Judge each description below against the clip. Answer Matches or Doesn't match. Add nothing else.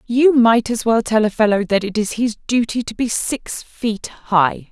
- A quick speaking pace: Matches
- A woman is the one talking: Matches